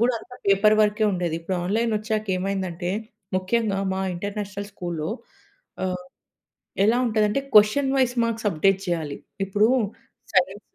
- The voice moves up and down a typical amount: Yes, average, 3.0 semitones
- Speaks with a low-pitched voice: No, high, 205 Hz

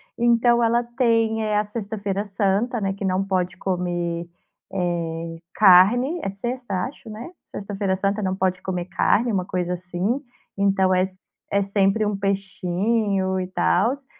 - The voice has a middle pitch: No, high, 195 Hz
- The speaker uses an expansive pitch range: No, average, 3.2 semitones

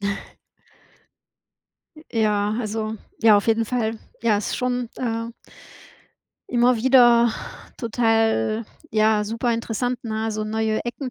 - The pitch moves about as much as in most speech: No, narrow, 1.7 semitones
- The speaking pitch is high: Yes, high, 225 Hz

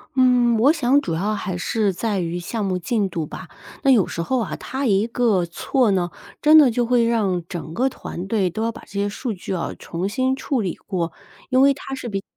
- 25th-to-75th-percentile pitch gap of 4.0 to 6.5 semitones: Yes, wide, 5.4 semitones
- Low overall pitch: No, high, 215 Hz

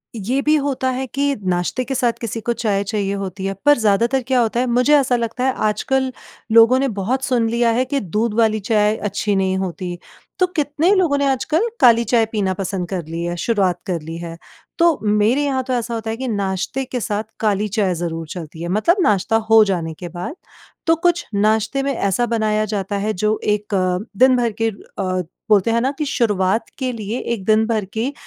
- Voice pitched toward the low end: No, high, 220 Hz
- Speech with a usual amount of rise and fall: Yes, average, 4.6 semitones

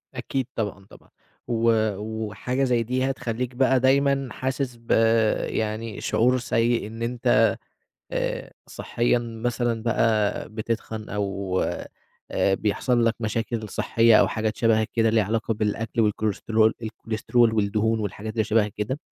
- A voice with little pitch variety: Yes, narrow, 2.0 semitones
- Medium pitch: No, low, 115 Hz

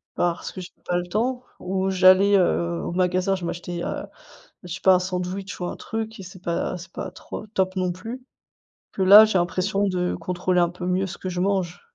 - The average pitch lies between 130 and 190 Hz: Yes, medium, 185 Hz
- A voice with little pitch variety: Yes, narrow, 1.5 semitones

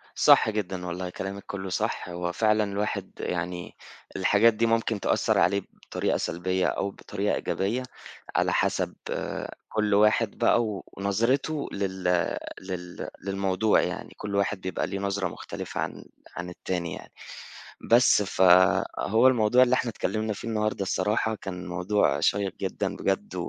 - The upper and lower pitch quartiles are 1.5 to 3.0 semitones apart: Yes, narrow, 2.6 semitones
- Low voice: Yes, low, 100 Hz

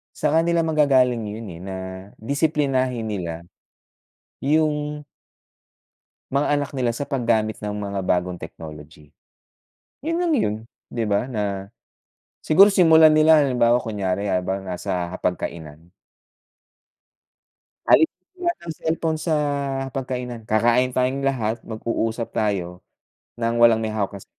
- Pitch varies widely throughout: Yes, wide, 6.6 semitones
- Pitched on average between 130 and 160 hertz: No, low, 115 Hz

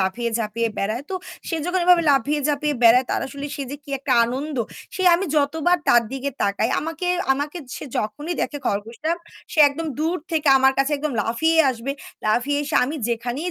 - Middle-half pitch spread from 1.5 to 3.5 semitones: No, average, 4.9 semitones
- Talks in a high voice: Yes, very high, 280 Hz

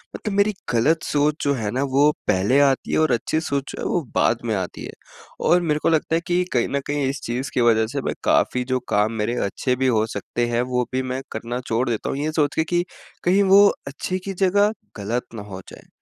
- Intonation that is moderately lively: Yes, average, 5.0 semitones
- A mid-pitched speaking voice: No, low, 130 Hz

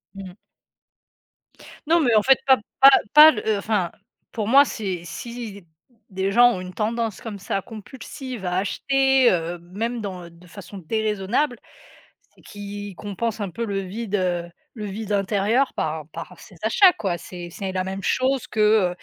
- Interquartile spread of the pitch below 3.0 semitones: No, average, 4.0 semitones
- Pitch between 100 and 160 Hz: No, high, 205 Hz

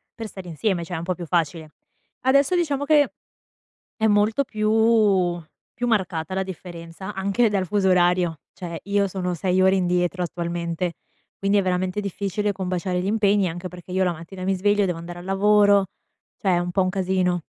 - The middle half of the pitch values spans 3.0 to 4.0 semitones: No, narrow, 2.6 semitones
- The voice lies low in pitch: No, medium, 185 Hz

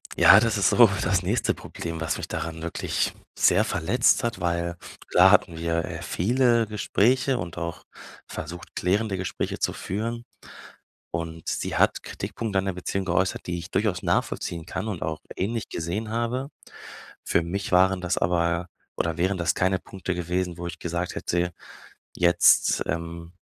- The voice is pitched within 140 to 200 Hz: No, very low, 90 Hz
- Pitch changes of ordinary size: Yes, average, 3.2 semitones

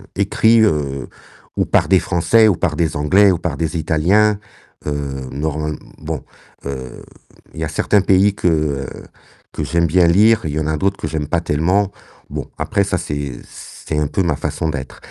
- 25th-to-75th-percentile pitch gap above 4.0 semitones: Yes, average, 4.5 semitones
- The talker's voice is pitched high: No, very low, 80 Hz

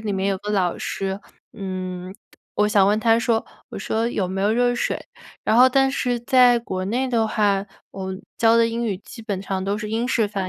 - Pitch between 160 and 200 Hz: No, high, 210 Hz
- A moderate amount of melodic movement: Yes, average, 3.2 semitones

